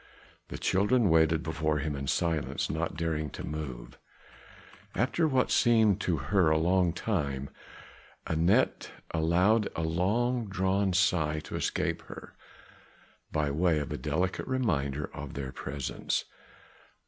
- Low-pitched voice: Yes, very low, 80 Hz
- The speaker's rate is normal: No, slow, 130 wpm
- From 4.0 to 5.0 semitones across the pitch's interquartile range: Yes, average, 4.5 semitones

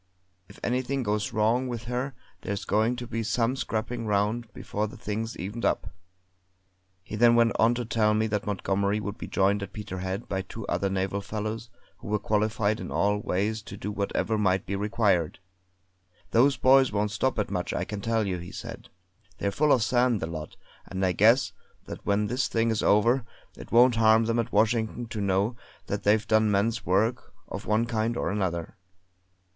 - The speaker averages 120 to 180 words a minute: No, average, 190 wpm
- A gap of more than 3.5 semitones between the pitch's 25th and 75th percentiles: No, narrow, 2.6 semitones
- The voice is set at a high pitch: No, low, 110 Hz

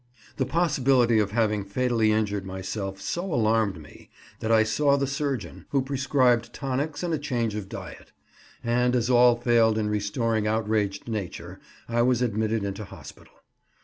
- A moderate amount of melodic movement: Yes, average, 3.3 semitones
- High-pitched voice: No, low, 115 Hz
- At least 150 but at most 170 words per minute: Yes, average, 155 wpm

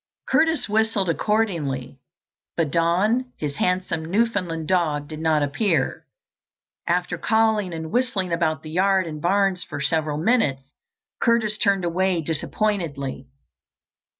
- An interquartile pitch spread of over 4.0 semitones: Yes, average, 5.0 semitones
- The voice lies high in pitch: No, medium, 175 Hz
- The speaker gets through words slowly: Yes, slow, 120 wpm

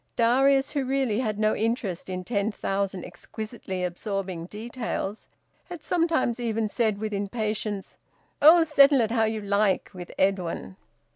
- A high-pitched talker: Yes, high, 215 Hz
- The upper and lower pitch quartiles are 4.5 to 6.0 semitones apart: No, average, 3.9 semitones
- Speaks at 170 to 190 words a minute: No, average, 140 wpm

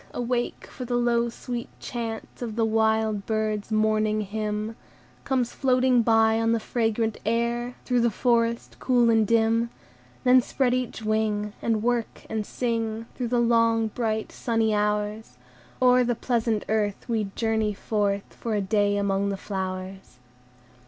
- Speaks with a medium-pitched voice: No, high, 225 Hz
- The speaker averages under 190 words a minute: Yes, average, 150 wpm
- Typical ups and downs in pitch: No, narrow, 1.9 semitones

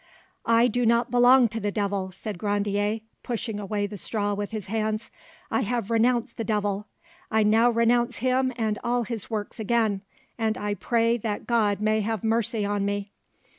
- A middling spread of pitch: No, narrow, 2.2 semitones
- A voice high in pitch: Yes, high, 220 Hz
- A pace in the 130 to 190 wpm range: Yes, average, 175 wpm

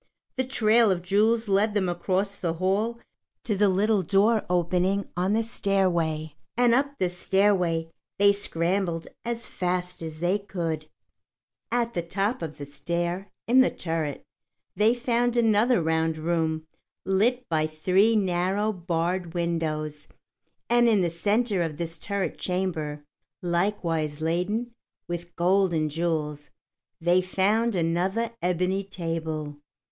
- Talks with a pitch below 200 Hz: Yes, medium, 185 Hz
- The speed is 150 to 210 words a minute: No, slow, 135 wpm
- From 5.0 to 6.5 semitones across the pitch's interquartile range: No, average, 4.0 semitones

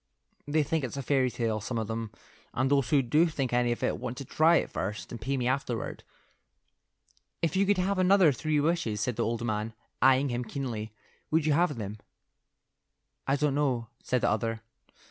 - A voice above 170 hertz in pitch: No, low, 130 Hz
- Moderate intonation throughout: Yes, average, 4.6 semitones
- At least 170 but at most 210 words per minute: Yes, average, 200 wpm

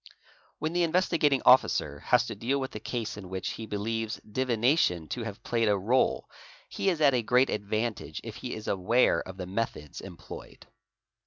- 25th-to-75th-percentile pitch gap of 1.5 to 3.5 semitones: No, average, 4.1 semitones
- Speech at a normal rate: Yes, average, 180 wpm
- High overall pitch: No, low, 115 Hz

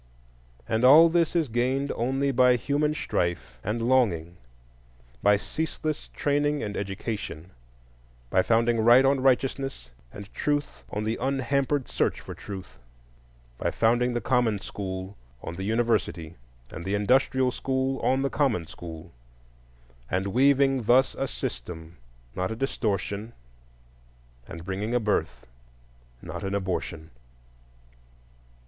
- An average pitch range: No, wide, 5.7 semitones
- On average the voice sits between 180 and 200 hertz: No, low, 115 Hz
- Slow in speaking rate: Yes, slow, 125 wpm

